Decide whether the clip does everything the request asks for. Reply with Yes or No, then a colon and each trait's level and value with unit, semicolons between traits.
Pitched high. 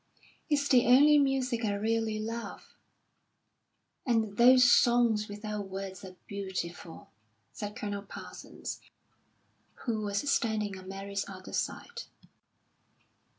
Yes: high, 215 Hz